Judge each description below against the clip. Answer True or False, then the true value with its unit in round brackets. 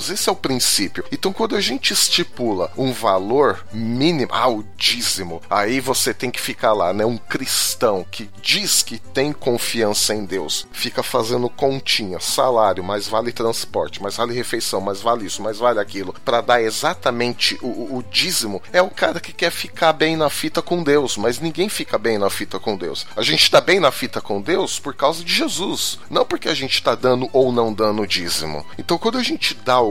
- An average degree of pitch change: False (6.7 semitones)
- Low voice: True (120 Hz)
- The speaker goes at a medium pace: False (205 wpm)